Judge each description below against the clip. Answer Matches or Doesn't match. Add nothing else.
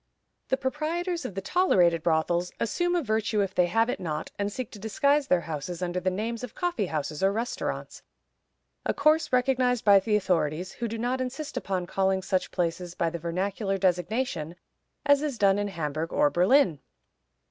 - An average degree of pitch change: Doesn't match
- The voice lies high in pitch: Matches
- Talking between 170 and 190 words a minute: Matches